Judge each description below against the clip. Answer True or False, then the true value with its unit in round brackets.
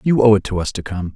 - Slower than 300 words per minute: False (365 wpm)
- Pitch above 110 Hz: False (105 Hz)